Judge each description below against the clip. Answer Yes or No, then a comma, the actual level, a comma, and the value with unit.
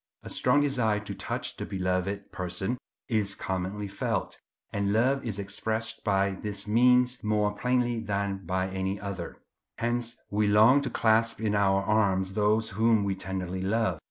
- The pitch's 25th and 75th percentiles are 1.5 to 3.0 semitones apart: Yes, narrow, 2.6 semitones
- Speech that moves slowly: No, average, 155 wpm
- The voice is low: Yes, low, 105 Hz